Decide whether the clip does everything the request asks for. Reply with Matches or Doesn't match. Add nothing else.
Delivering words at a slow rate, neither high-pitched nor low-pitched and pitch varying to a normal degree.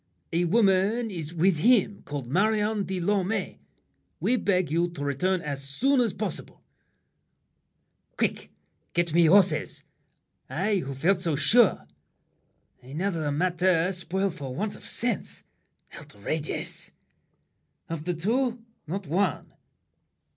Matches